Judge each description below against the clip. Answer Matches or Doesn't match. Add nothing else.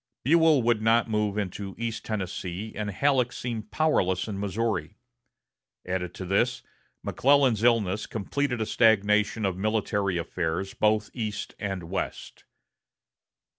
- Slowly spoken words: Matches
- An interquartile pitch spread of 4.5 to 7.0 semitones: Doesn't match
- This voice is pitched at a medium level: Doesn't match